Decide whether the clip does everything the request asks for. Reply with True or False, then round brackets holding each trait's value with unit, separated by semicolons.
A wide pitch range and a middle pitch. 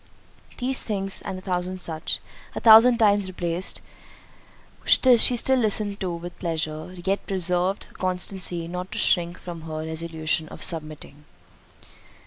False (3.2 semitones; 180 Hz)